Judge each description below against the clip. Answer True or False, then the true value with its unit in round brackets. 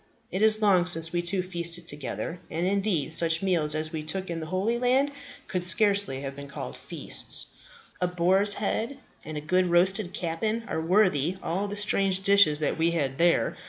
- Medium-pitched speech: True (180 Hz)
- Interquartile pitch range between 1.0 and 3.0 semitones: False (3.5 semitones)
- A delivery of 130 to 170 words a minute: False (190 wpm)